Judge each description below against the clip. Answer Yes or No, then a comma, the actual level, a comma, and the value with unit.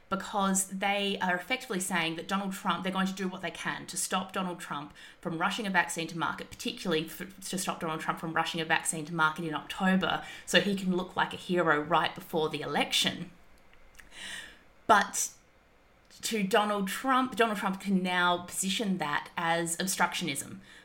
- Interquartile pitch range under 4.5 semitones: Yes, average, 2.7 semitones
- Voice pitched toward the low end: No, medium, 180 Hz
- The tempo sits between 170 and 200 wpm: Yes, average, 180 wpm